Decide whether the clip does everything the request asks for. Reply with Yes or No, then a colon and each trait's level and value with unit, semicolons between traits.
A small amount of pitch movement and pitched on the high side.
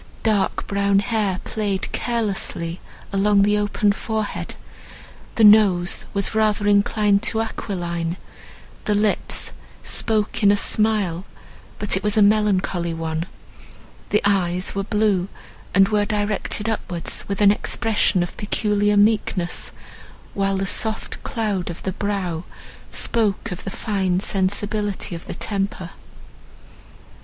Yes: narrow, 2.0 semitones; high, 200 Hz